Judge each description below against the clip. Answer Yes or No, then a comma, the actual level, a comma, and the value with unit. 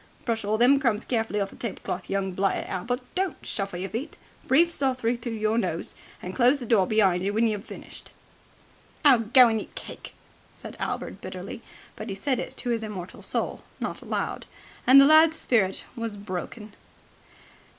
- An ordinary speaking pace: Yes, average, 175 wpm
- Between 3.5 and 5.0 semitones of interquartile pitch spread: Yes, average, 3.9 semitones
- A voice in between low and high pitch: No, high, 225 Hz